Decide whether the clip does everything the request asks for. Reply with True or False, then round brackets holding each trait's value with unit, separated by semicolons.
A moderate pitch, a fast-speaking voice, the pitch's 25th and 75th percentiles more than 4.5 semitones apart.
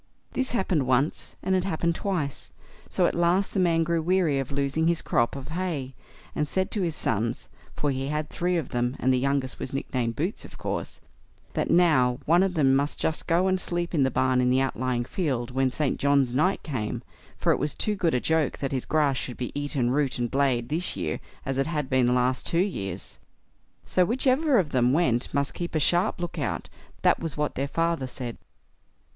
True (145 Hz; 210 wpm; 4.9 semitones)